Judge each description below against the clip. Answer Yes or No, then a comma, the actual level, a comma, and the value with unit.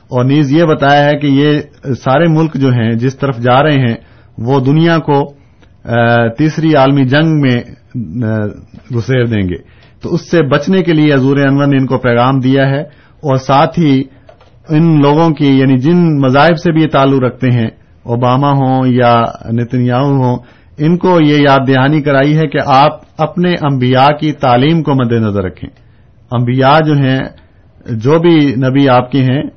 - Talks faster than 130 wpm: Yes, average, 175 wpm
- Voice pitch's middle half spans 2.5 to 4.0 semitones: Yes, average, 3.5 semitones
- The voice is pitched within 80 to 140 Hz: Yes, low, 135 Hz